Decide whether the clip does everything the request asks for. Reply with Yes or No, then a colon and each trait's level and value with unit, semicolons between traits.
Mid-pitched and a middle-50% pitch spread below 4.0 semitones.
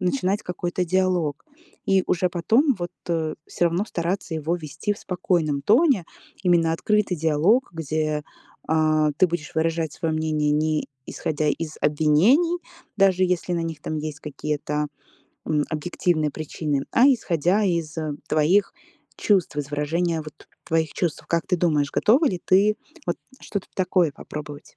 Yes: medium, 165 Hz; average, 3.3 semitones